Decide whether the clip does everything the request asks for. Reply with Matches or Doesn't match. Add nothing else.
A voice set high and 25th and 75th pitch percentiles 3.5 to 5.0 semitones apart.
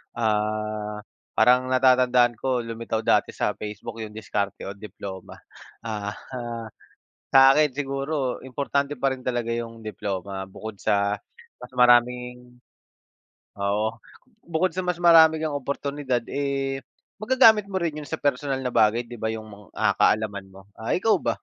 Doesn't match